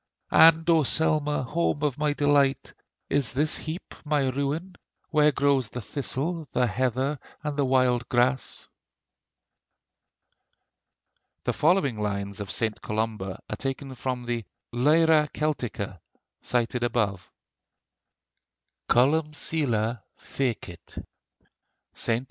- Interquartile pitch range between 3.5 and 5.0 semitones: Yes, average, 4.0 semitones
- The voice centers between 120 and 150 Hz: Yes, low, 135 Hz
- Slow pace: Yes, slow, 105 wpm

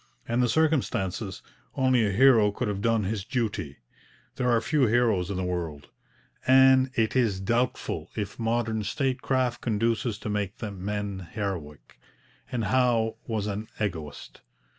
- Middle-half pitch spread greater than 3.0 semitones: Yes, average, 3.7 semitones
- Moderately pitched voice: No, low, 110 Hz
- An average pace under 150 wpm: Yes, average, 140 wpm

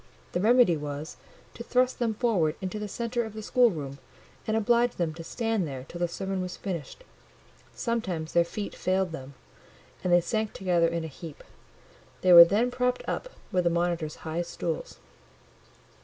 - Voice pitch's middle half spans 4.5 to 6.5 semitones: Yes, average, 5.0 semitones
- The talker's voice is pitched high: No, medium, 180 Hz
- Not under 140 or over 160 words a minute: No, average, 170 wpm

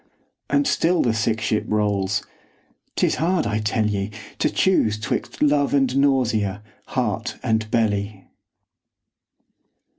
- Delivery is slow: Yes, slow, 120 wpm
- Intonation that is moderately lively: Yes, average, 4.7 semitones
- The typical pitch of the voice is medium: No, low, 110 Hz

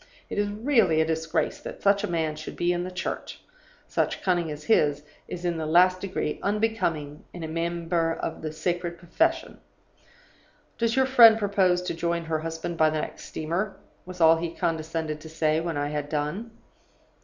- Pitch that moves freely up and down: No, average, 2.8 semitones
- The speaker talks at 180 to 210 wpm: Yes, average, 185 wpm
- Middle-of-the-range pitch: Yes, medium, 170 Hz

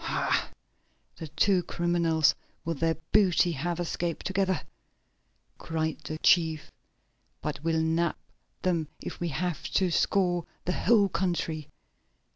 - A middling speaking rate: No, slow, 120 wpm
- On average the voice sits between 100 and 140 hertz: No, medium, 170 Hz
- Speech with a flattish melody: Yes, narrow, 2.1 semitones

